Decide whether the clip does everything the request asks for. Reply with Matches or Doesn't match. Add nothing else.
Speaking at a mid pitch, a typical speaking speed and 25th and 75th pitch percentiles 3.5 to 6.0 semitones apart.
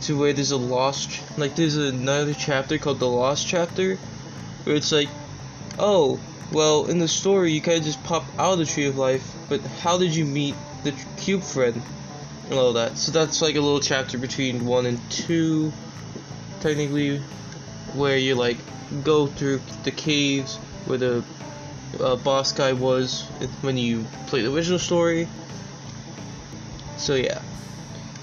Doesn't match